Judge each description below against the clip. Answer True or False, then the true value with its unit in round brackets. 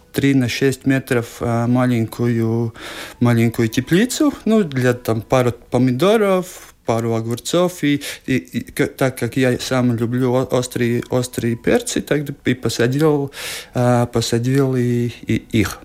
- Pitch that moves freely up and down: False (2.7 semitones)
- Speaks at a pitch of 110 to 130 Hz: True (125 Hz)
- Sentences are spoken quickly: False (130 wpm)